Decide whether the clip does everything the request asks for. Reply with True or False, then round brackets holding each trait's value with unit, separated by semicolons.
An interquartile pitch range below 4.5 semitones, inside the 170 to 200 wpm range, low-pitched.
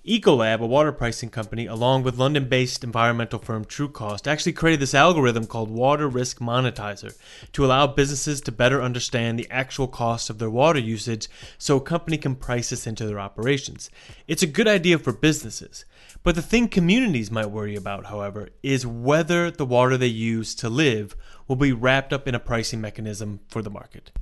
True (4.1 semitones; 185 wpm; 125 Hz)